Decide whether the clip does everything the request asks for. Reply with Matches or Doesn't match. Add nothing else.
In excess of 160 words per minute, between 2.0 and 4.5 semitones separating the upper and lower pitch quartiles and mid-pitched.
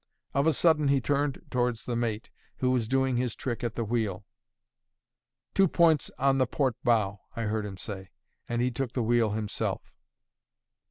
Doesn't match